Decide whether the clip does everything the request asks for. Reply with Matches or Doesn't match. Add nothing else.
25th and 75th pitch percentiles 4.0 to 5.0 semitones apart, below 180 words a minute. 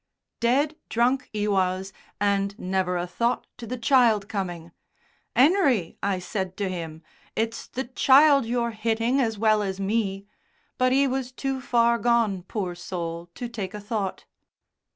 Matches